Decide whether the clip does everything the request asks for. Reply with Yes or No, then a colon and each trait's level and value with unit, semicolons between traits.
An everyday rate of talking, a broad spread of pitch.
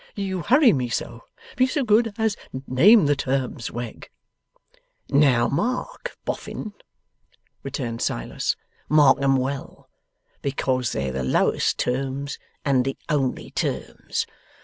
No: slow, 120 wpm; wide, 7.8 semitones